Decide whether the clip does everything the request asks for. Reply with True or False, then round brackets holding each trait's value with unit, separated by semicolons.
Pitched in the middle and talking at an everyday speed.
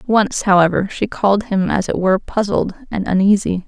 False (200 Hz; 180 wpm)